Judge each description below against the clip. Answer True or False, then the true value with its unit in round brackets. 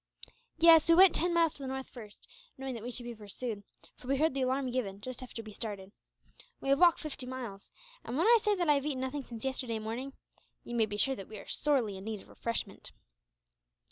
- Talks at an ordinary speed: False (235 wpm)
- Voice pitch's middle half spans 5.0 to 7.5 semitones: False (4.2 semitones)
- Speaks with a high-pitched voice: True (255 Hz)